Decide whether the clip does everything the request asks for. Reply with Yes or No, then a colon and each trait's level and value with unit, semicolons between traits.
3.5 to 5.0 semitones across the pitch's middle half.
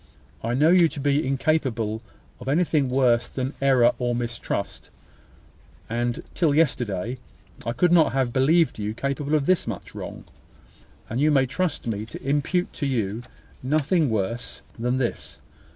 Yes: average, 3.9 semitones